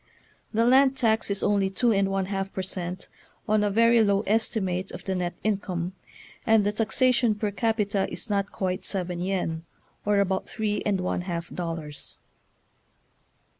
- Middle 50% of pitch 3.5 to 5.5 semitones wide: No, average, 2.8 semitones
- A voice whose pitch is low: No, high, 200 Hz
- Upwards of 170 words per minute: No, average, 165 wpm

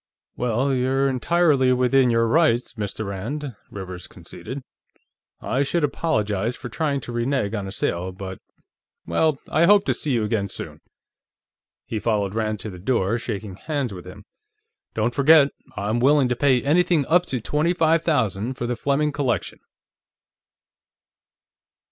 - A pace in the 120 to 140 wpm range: No, average, 150 wpm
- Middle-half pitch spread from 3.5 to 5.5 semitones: Yes, average, 5.2 semitones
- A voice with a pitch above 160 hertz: No, low, 125 Hz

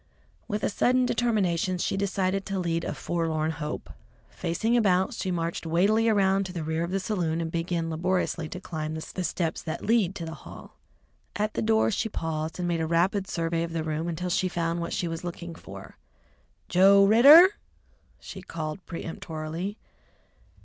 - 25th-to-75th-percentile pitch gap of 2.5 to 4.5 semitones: Yes, average, 3.1 semitones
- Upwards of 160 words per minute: Yes, average, 175 wpm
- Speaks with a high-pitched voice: No, medium, 175 Hz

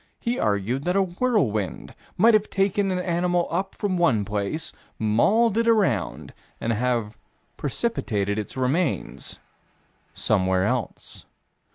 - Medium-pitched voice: Yes, medium, 160 Hz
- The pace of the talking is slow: Yes, slow, 125 wpm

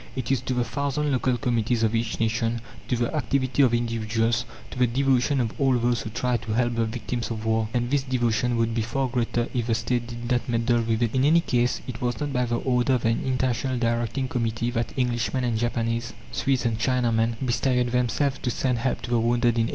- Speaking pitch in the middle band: No, low, 120 Hz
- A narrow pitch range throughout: Yes, narrow, 1.7 semitones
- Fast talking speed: Yes, fast, 230 wpm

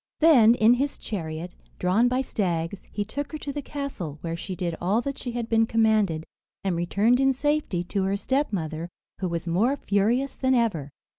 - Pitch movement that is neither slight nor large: No, wide, 6.7 semitones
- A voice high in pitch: Yes, high, 215 Hz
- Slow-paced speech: No, average, 190 wpm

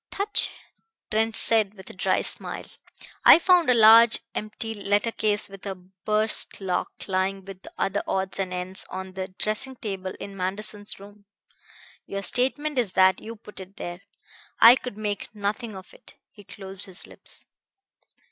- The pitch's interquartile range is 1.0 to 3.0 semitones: Yes, narrow, 2.6 semitones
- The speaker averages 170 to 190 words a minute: No, average, 160 wpm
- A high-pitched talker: Yes, high, 205 Hz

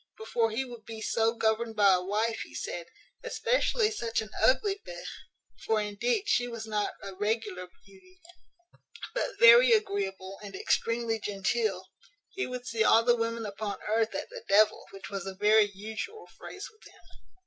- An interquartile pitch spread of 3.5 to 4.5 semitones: No, average, 3.1 semitones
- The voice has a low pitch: No, high, 220 Hz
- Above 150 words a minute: Yes, average, 170 wpm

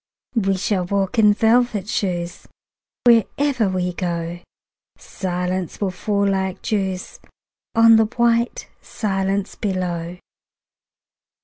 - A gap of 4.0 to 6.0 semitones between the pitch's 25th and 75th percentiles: No, average, 3.4 semitones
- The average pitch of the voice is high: Yes, high, 195 Hz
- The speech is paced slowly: Yes, slow, 95 wpm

